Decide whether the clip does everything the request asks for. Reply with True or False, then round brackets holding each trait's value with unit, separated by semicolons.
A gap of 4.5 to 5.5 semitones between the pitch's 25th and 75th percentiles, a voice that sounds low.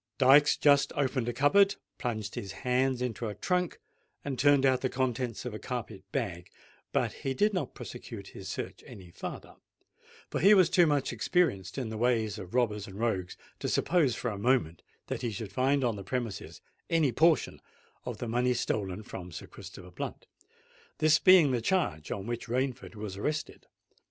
True (5.2 semitones; 125 Hz)